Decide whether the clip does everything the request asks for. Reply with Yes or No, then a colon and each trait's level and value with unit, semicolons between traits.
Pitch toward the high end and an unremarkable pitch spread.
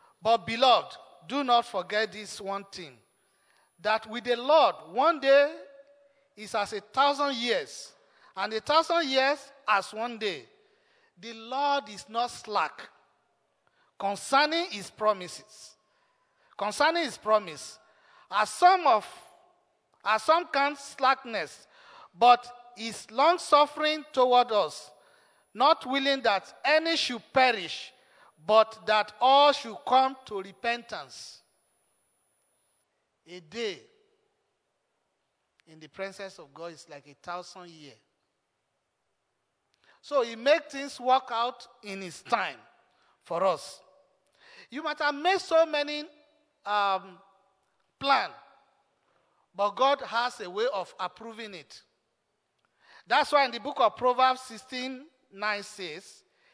No: very high, 255 Hz; wide, 6.1 semitones